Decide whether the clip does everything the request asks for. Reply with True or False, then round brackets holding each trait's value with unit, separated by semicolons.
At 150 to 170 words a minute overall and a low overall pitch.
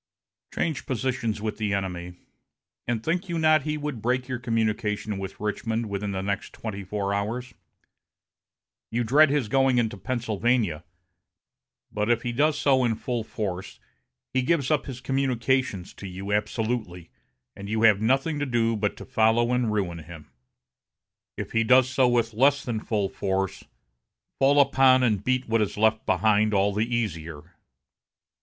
True (160 wpm; 115 Hz)